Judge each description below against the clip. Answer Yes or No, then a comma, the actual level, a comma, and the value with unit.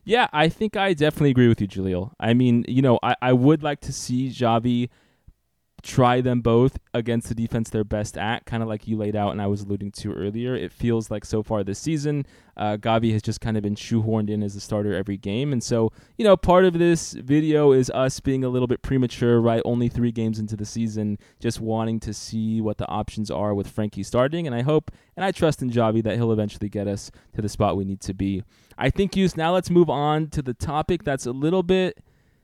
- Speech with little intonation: No, average, 4.3 semitones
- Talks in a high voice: No, low, 115 Hz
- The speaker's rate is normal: No, fast, 240 wpm